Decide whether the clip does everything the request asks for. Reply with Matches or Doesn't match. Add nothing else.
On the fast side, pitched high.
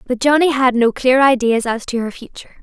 Matches